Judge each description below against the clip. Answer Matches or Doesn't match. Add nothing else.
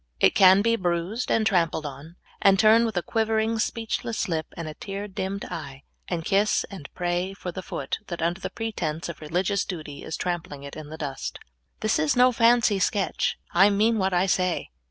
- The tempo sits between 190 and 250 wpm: Matches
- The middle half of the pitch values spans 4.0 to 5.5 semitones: Matches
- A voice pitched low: Doesn't match